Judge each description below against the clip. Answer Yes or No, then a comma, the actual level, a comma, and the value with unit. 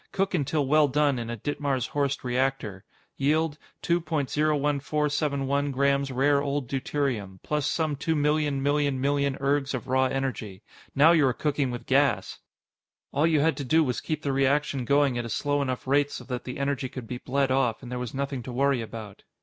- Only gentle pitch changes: Yes, narrow, 2.3 semitones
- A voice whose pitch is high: No, medium, 140 Hz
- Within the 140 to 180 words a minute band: No, average, 190 wpm